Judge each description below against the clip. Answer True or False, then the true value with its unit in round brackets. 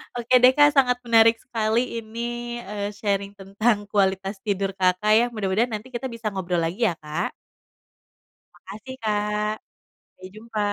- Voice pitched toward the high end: True (210 Hz)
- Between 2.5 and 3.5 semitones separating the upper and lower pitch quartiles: True (3.0 semitones)